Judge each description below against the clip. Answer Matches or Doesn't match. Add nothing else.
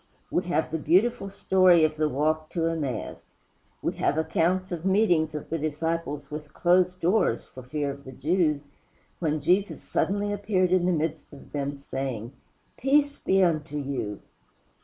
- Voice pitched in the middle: Matches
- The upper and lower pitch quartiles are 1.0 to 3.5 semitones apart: Doesn't match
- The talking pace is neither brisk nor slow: Matches